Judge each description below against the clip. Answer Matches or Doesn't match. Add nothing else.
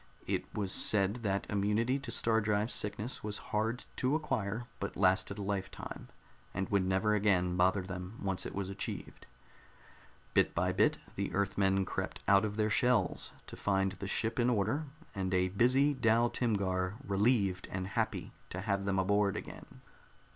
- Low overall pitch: Matches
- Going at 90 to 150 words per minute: Doesn't match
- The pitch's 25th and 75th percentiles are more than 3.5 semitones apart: Doesn't match